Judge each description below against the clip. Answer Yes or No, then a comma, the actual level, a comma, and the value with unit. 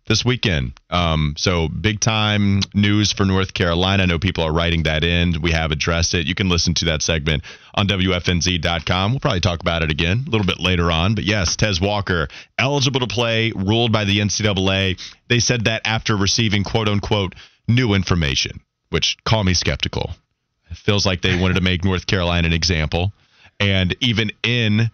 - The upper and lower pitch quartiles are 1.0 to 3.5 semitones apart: No, average, 3.9 semitones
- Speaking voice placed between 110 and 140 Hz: No, very low, 95 Hz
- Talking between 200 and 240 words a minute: No, average, 190 wpm